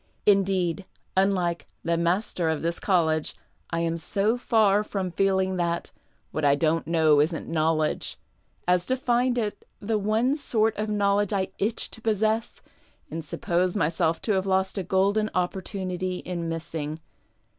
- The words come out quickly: No, average, 160 wpm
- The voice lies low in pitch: No, medium, 185 Hz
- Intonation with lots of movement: No, average, 3.7 semitones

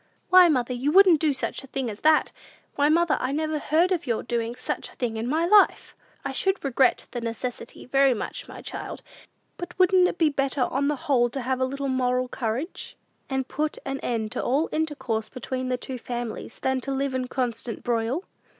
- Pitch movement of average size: Yes, average, 3.7 semitones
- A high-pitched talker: Yes, very high, 265 Hz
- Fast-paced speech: Yes, fast, 210 wpm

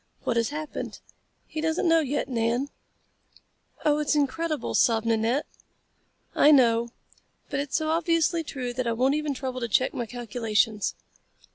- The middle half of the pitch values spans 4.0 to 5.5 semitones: Yes, average, 4.6 semitones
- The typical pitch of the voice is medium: No, very high, 265 Hz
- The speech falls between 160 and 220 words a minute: No, average, 150 wpm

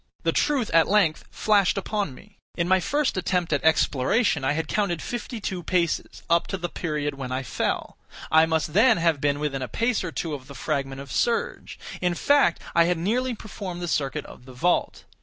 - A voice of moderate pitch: Yes, medium, 170 Hz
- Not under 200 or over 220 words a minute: Yes, fast, 205 wpm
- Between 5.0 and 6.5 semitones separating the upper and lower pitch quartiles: Yes, wide, 5.4 semitones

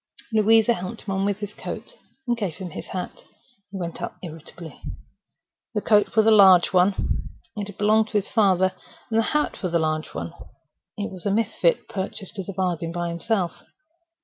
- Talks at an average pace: Yes, average, 185 wpm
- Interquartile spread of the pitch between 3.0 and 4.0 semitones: Yes, average, 3.3 semitones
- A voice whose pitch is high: Yes, high, 195 Hz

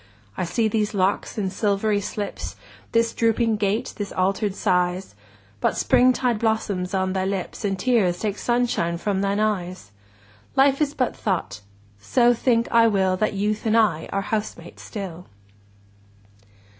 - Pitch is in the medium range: No, high, 205 Hz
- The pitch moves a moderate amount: Yes, average, 3.4 semitones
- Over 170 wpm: No, average, 150 wpm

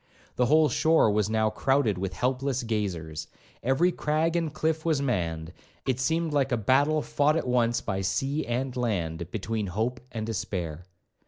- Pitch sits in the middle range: No, low, 120 Hz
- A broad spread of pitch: Yes, wide, 6.1 semitones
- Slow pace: No, average, 165 wpm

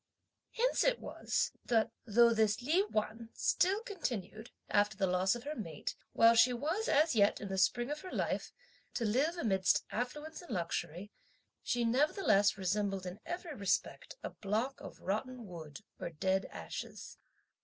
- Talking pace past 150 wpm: Yes, average, 160 wpm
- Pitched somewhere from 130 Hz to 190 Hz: No, high, 230 Hz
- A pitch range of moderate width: No, wide, 7.0 semitones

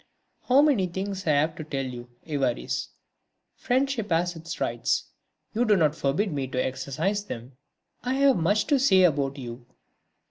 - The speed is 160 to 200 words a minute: Yes, average, 165 wpm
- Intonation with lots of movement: Yes, wide, 7.2 semitones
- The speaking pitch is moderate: Yes, medium, 170 Hz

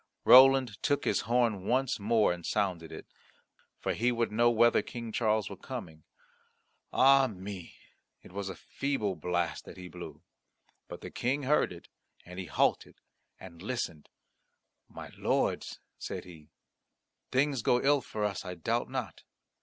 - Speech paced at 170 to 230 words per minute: No, average, 155 wpm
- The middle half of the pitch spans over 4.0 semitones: Yes, wide, 5.5 semitones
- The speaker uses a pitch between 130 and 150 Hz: No, low, 110 Hz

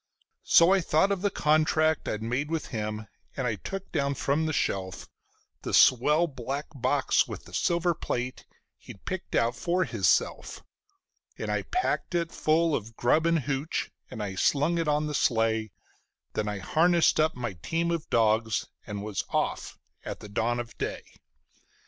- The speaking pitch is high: No, medium, 145 Hz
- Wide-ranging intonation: Yes, wide, 6.5 semitones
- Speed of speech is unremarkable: Yes, average, 165 wpm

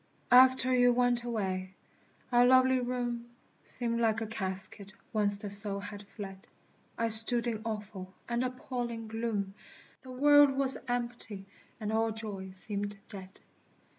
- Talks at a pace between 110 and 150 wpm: Yes, slow, 135 wpm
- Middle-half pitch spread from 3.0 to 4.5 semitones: Yes, average, 3.3 semitones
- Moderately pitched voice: No, high, 225 Hz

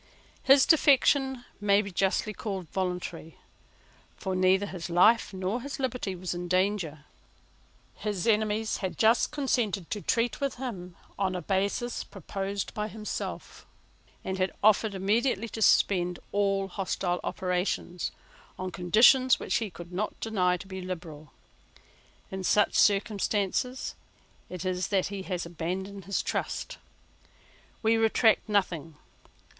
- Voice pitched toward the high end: Yes, high, 195 Hz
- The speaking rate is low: Yes, slow, 130 wpm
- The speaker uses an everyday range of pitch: Yes, average, 3.2 semitones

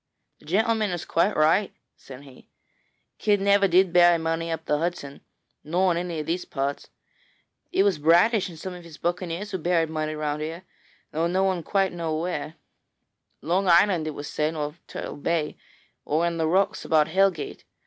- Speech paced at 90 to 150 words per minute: No, average, 180 wpm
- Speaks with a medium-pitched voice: Yes, medium, 170 Hz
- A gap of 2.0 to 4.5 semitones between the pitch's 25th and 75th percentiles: Yes, average, 3.2 semitones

